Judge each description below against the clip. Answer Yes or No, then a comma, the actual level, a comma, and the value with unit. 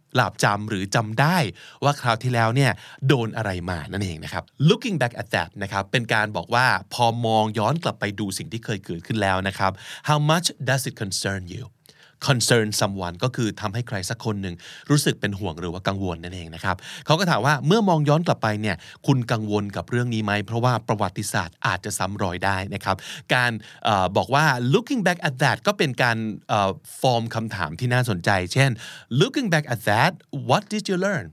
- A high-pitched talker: No, low, 115 Hz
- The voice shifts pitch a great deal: Yes, wide, 5.8 semitones